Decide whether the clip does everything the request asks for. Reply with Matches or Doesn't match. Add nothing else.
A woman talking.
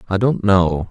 Doesn't match